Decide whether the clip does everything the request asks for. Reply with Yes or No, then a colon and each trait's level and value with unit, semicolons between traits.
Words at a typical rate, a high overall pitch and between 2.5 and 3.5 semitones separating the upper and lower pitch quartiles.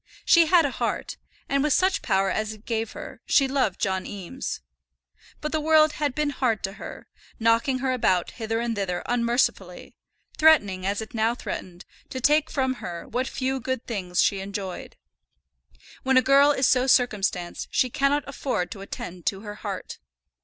No: average, 175 wpm; high, 240 Hz; wide, 5.5 semitones